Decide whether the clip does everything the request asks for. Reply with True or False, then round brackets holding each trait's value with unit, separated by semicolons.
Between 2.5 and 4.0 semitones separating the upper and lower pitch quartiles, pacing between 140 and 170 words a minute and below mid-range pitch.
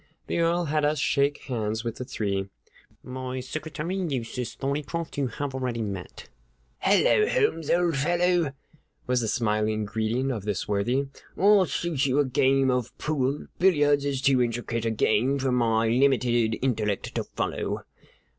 False (4.5 semitones; 155 wpm; 130 Hz)